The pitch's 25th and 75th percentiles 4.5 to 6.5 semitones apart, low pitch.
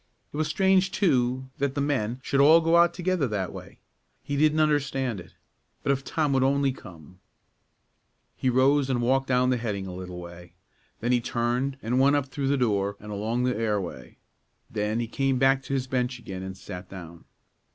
Yes: average, 4.9 semitones; low, 125 Hz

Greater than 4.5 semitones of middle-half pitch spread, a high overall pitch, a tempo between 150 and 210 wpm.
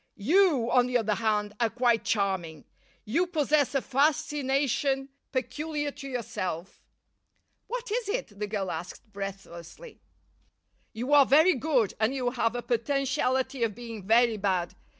No: average, 5.1 semitones; high, 245 Hz; average, 140 wpm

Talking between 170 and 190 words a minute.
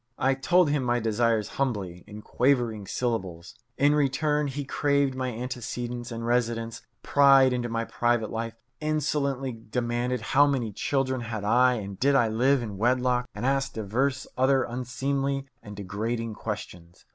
No: average, 150 wpm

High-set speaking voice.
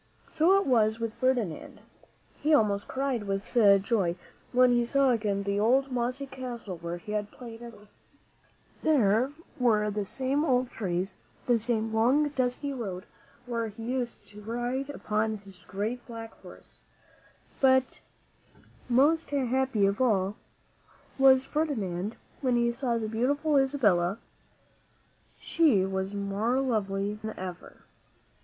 Yes: high, 235 Hz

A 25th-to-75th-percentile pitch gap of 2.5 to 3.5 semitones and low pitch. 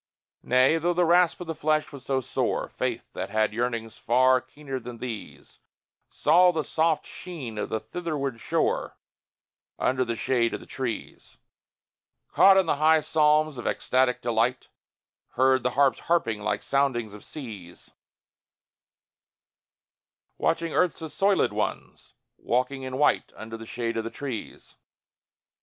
No: average, 5.0 semitones; low, 130 Hz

